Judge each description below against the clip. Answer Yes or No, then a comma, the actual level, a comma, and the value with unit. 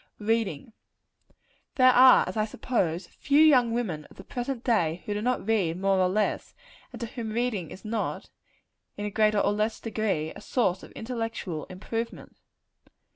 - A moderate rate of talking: Yes, average, 170 wpm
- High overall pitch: Yes, high, 215 Hz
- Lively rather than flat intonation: No, average, 3.8 semitones